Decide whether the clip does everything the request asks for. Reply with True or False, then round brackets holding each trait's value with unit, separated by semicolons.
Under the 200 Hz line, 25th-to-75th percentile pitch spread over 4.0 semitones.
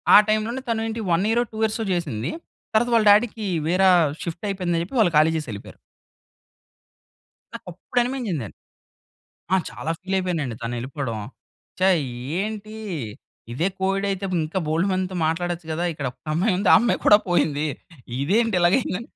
True (185 Hz; 5.0 semitones)